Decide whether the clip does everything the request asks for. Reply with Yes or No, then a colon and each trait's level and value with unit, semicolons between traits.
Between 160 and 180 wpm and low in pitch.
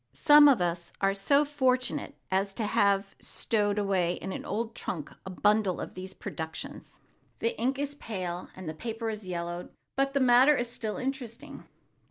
No: average, 170 wpm; high, 215 Hz